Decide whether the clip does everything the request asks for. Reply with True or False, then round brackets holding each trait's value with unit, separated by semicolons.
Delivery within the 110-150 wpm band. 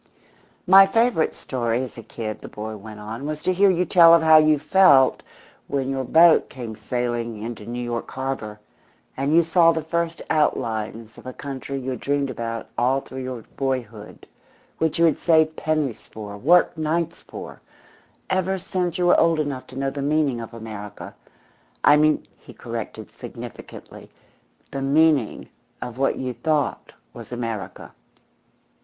False (165 wpm)